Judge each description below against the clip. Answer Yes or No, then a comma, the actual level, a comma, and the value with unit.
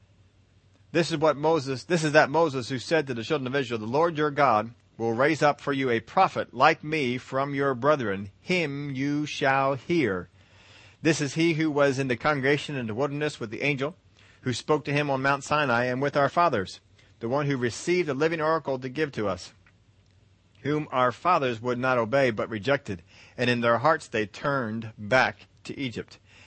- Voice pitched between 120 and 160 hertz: Yes, low, 135 Hz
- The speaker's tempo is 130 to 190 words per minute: No, average, 200 wpm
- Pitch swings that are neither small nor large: No, wide, 5.7 semitones